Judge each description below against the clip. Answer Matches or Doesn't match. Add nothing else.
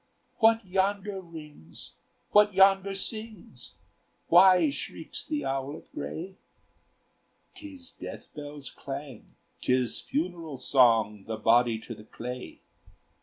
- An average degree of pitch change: Doesn't match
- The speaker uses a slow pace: Matches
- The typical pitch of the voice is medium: Matches